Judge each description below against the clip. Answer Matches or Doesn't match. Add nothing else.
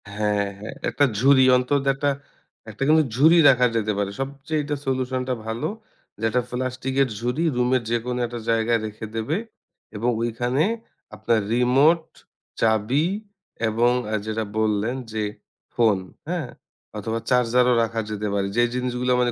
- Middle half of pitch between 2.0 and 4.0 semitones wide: Matches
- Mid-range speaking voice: Doesn't match